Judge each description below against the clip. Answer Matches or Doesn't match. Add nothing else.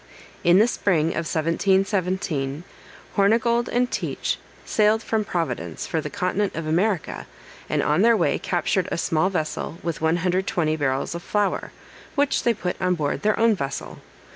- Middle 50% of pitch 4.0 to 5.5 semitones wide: Matches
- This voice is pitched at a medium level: Matches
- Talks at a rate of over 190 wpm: Doesn't match